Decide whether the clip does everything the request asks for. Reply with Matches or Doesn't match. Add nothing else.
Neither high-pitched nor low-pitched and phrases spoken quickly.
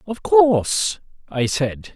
Doesn't match